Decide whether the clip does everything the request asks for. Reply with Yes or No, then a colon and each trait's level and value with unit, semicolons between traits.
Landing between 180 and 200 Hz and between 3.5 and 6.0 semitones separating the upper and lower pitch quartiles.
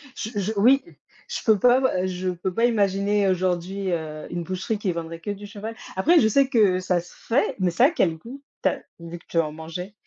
Yes: high, 190 Hz; average, 3.8 semitones